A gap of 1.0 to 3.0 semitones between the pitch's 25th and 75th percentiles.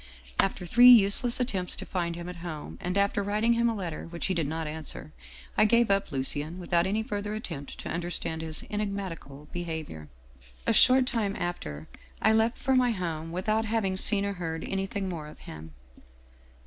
No: average, 4.7 semitones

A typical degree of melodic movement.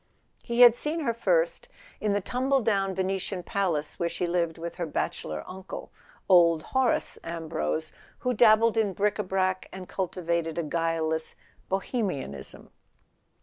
Yes: average, 4.7 semitones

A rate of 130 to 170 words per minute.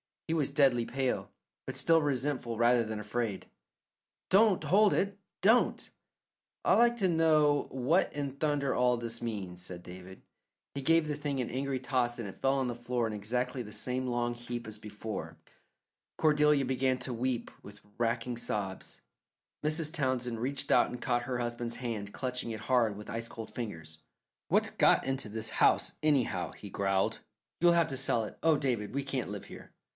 No: average, 180 wpm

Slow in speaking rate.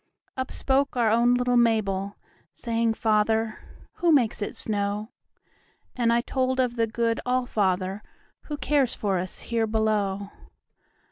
Yes: slow, 125 wpm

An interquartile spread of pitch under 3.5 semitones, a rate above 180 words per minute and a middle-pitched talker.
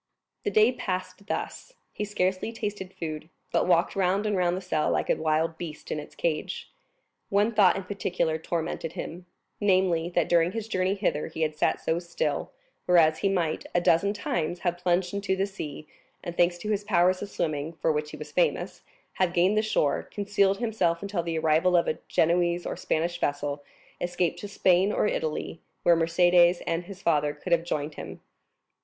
Yes: average, 3.1 semitones; average, 190 wpm; medium, 175 Hz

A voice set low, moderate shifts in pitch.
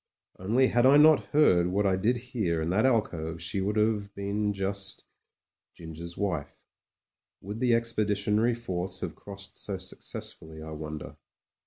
Yes: low, 100 Hz; average, 4.5 semitones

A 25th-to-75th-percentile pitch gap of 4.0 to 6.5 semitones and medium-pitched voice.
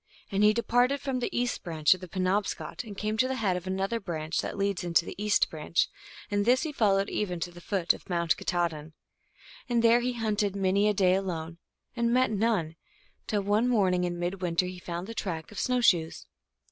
No: average, 4.4 semitones; high, 195 Hz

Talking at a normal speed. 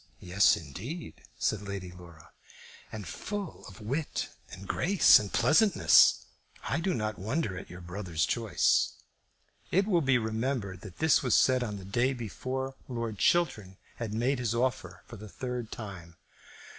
Yes: average, 155 wpm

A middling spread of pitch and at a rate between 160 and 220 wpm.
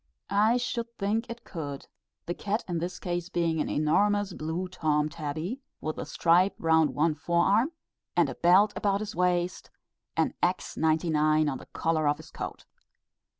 Yes: average, 4.3 semitones; average, 165 wpm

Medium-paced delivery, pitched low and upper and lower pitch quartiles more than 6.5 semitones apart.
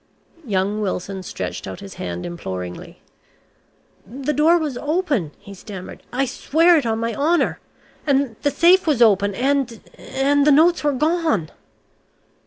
No: average, 145 wpm; very high, 260 Hz; wide, 7.7 semitones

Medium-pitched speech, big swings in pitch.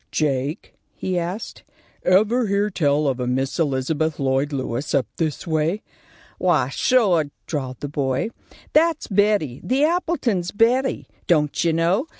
Yes: medium, 165 Hz; wide, 6.9 semitones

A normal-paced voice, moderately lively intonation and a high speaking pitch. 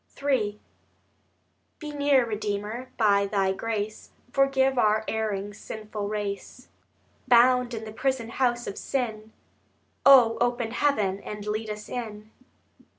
No: slow, 120 wpm; average, 3.2 semitones; high, 220 Hz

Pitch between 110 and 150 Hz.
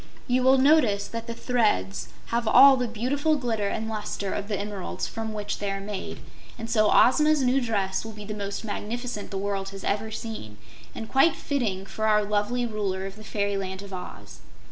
No: high, 215 Hz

